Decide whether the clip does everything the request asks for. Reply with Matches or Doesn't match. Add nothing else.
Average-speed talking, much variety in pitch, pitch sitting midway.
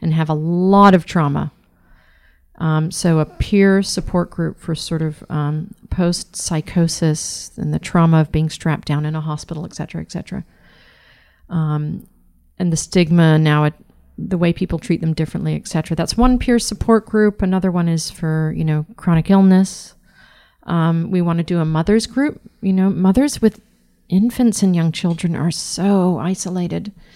Doesn't match